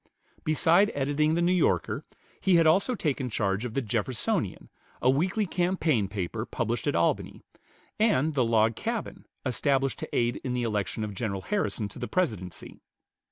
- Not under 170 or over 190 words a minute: No, average, 160 wpm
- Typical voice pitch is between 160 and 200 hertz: No, low, 130 Hz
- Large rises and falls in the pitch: Yes, wide, 7.2 semitones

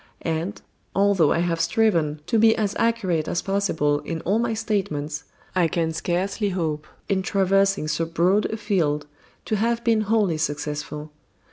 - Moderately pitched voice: Yes, medium, 180 Hz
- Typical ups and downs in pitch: Yes, average, 4.8 semitones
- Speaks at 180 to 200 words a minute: No, average, 155 wpm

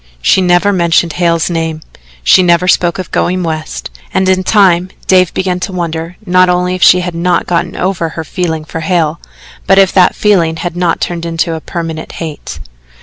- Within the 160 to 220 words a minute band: Yes, average, 185 wpm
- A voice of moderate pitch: Yes, medium, 175 Hz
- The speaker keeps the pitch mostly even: Yes, narrow, 1.8 semitones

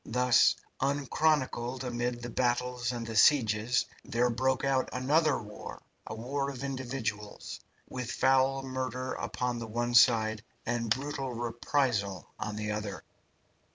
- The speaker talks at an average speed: No, slow, 130 wpm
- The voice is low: Yes, low, 125 Hz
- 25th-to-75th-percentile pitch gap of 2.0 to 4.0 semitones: Yes, narrow, 2.4 semitones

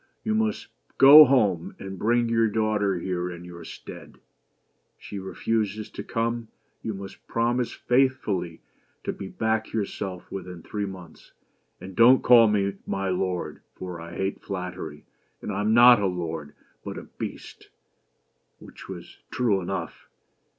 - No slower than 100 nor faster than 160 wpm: Yes, average, 150 wpm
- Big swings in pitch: No, average, 4.1 semitones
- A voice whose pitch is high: No, low, 100 Hz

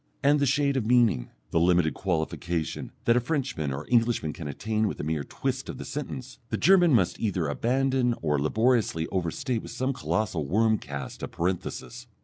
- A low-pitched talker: Yes, low, 110 Hz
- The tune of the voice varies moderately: No, wide, 7.9 semitones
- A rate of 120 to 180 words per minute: Yes, average, 175 wpm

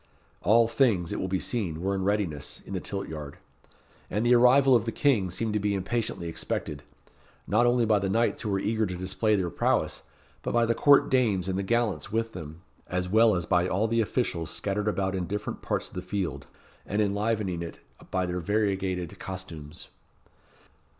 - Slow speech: No, average, 195 wpm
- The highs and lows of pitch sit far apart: No, average, 3.7 semitones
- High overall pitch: No, low, 100 Hz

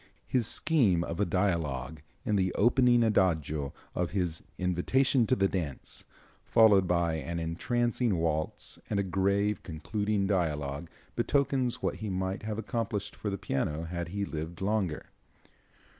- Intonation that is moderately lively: Yes, average, 4.5 semitones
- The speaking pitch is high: No, very low, 95 Hz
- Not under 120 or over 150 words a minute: Yes, average, 145 wpm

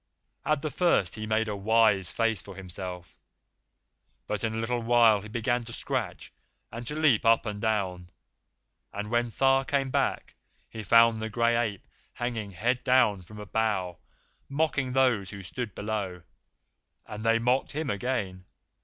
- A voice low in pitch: Yes, low, 110 Hz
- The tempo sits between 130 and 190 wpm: Yes, average, 165 wpm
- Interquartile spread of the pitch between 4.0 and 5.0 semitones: No, average, 3.1 semitones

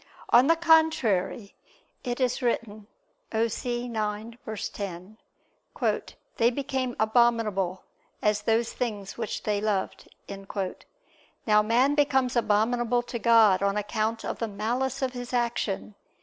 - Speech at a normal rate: No, slow, 115 wpm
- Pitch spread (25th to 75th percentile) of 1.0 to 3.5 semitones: Yes, average, 2.7 semitones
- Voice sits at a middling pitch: No, high, 230 Hz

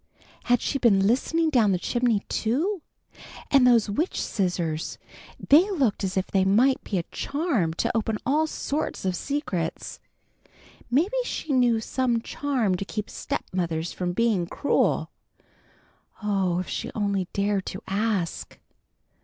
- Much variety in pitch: Yes, wide, 6.1 semitones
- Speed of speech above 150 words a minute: No, average, 140 wpm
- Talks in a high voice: Yes, high, 220 Hz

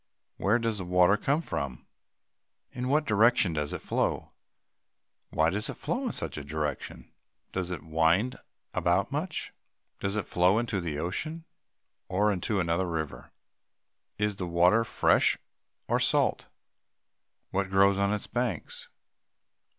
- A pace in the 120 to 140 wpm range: Yes, slow, 135 wpm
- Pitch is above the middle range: No, very low, 95 Hz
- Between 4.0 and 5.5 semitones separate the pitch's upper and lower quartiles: Yes, average, 4.8 semitones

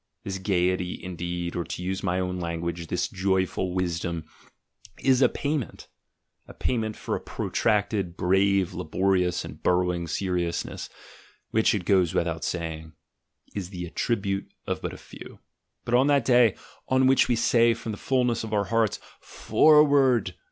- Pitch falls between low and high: No, very low, 95 Hz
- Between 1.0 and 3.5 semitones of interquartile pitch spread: No, average, 4.6 semitones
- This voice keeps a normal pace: Yes, average, 160 wpm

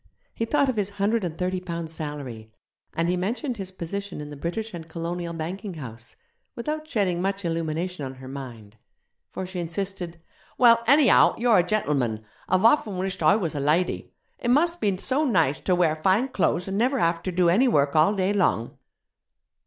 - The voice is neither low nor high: Yes, medium, 180 Hz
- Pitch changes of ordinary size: Yes, average, 4.5 semitones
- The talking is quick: No, average, 190 wpm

